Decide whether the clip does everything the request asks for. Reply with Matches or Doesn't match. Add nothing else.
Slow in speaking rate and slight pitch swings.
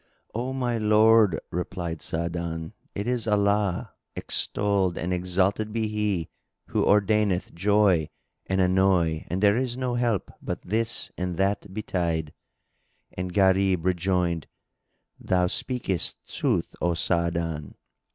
Doesn't match